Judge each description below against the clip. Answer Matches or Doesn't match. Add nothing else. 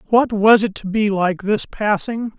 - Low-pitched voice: Doesn't match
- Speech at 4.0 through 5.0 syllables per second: Matches